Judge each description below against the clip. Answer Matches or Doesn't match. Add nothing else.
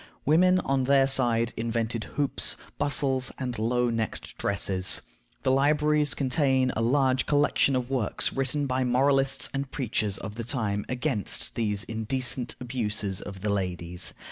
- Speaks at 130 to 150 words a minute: Matches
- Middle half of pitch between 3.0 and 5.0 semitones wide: Matches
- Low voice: Matches